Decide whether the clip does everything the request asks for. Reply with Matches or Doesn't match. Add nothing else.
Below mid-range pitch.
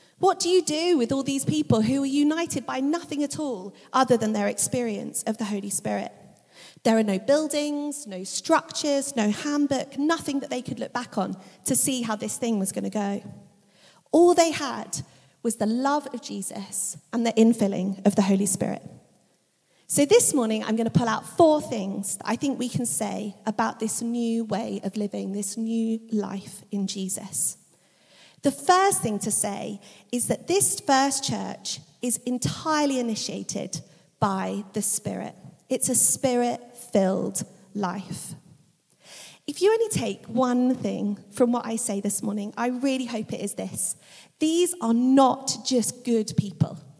Doesn't match